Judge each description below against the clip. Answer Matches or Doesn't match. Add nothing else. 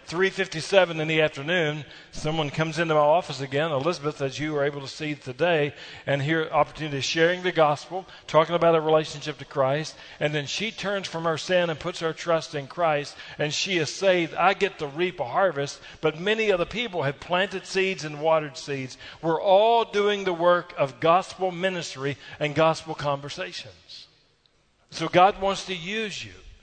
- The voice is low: Doesn't match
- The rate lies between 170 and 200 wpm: Matches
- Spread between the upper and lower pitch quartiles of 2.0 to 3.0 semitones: Doesn't match